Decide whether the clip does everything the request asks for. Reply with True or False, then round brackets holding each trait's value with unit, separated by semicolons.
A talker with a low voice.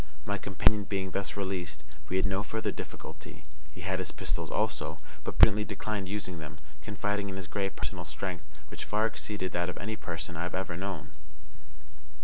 True (95 Hz)